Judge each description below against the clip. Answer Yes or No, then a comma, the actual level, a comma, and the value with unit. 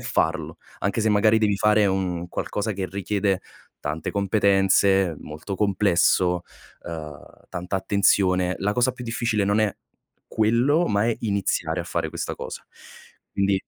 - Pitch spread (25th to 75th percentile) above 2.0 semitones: Yes, narrow, 2.4 semitones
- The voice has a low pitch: Yes, low, 100 Hz